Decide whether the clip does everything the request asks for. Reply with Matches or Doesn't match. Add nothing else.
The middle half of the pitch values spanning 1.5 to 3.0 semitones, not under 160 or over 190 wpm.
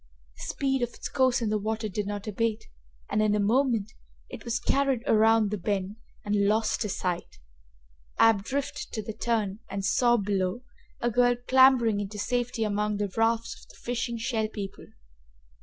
Matches